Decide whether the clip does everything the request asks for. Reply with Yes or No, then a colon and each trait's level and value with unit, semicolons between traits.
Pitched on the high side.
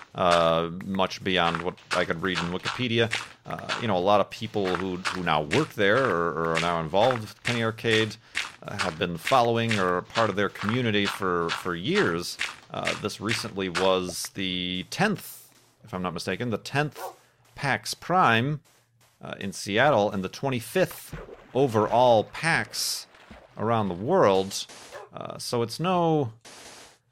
No: low, 105 Hz